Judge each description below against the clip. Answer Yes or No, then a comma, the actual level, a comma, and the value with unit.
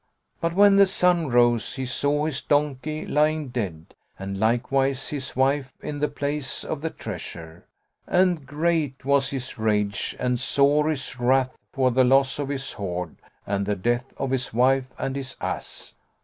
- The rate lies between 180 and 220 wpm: No, average, 165 wpm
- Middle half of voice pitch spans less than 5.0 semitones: Yes, average, 3.4 semitones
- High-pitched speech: No, low, 135 Hz